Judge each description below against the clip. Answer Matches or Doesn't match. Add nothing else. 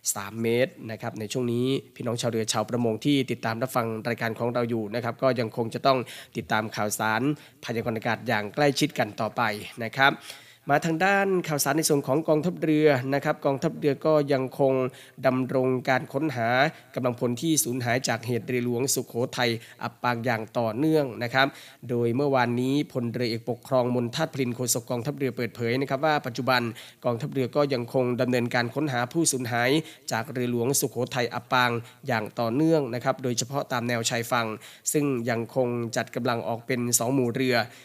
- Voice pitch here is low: Matches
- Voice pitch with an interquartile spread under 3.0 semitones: Matches